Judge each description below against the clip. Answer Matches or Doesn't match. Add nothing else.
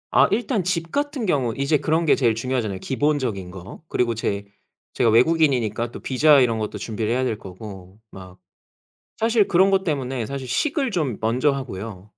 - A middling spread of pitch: Doesn't match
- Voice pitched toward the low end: Matches